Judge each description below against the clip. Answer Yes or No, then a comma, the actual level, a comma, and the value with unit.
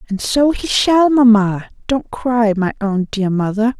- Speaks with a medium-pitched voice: No, high, 225 Hz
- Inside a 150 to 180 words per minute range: Yes, average, 175 wpm